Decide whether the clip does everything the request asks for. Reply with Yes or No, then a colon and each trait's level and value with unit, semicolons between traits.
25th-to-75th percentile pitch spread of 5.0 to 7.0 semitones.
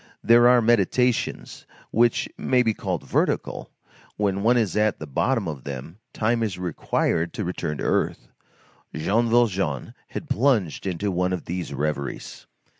Yes: wide, 5.6 semitones